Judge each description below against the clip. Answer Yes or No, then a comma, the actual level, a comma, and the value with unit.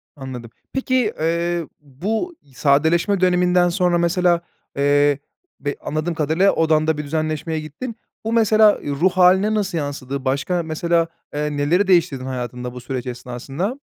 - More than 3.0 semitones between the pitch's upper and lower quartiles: Yes, average, 4.2 semitones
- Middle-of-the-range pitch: Yes, medium, 160 Hz